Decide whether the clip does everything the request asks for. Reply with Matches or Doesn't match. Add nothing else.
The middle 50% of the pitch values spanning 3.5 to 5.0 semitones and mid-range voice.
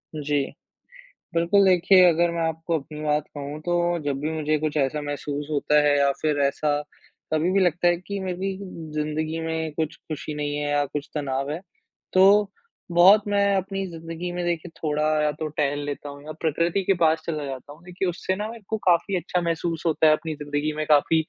Doesn't match